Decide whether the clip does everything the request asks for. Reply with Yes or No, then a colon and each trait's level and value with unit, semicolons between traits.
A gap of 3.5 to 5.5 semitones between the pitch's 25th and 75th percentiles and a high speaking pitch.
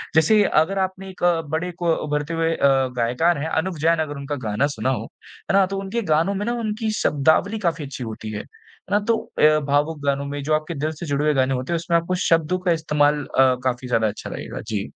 No: average, 4.2 semitones; medium, 155 Hz